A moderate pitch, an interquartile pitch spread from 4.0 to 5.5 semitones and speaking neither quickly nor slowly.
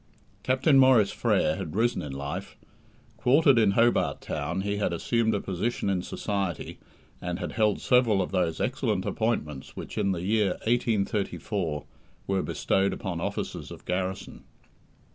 No: low, 100 Hz; average, 4.4 semitones; average, 145 wpm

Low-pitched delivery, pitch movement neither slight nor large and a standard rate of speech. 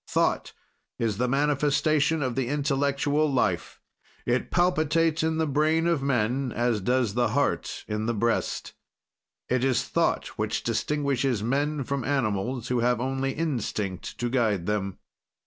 Yes: low, 130 Hz; average, 3.7 semitones; average, 145 wpm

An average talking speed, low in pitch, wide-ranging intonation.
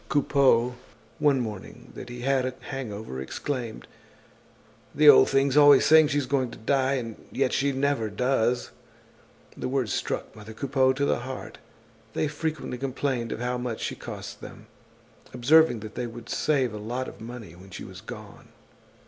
No: average, 165 wpm; low, 130 Hz; average, 3.1 semitones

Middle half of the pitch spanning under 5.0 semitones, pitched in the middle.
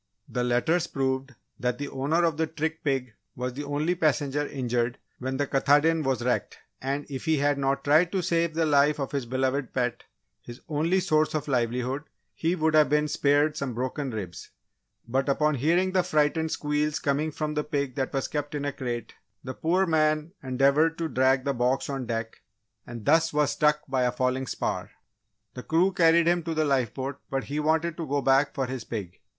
Yes: average, 3.1 semitones; medium, 145 Hz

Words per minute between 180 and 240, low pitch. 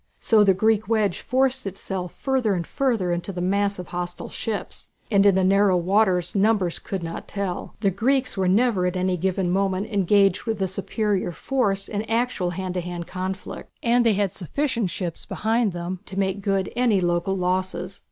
No: average, 185 wpm; high, 195 Hz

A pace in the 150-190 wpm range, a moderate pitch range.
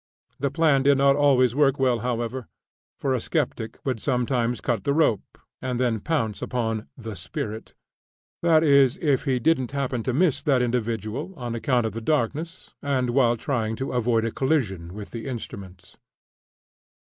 Yes: average, 165 wpm; average, 3.5 semitones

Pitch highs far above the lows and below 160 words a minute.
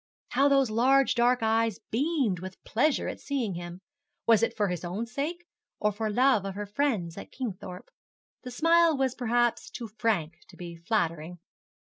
No: wide, 5.8 semitones; average, 170 wpm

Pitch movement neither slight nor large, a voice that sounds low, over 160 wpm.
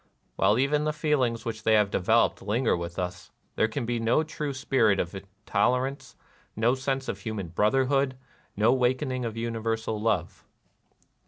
No: average, 3.7 semitones; low, 115 Hz; average, 155 wpm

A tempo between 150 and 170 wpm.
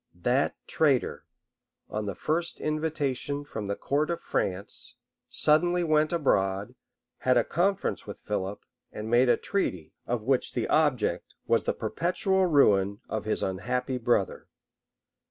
No: slow, 135 wpm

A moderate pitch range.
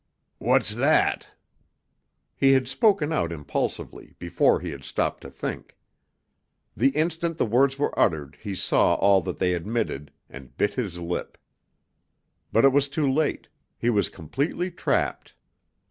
No: wide, 8.4 semitones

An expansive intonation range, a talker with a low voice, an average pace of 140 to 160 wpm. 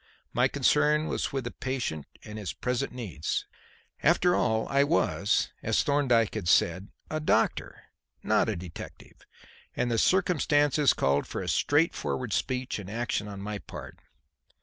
Yes: wide, 5.9 semitones; low, 125 Hz; average, 145 wpm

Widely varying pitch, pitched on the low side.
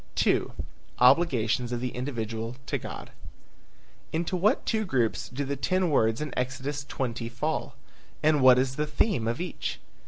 No: average, 3.9 semitones; low, 130 Hz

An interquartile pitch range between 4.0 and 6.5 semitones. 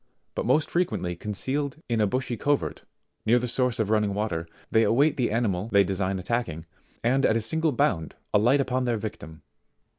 Yes: average, 4.5 semitones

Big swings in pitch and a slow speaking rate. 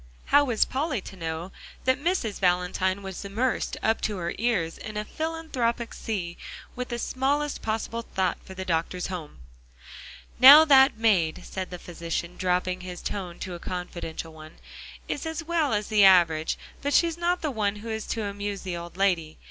No: wide, 6.0 semitones; average, 180 wpm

